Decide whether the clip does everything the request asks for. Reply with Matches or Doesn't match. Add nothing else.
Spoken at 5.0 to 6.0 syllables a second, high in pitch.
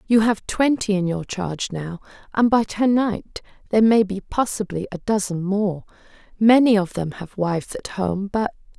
Doesn't match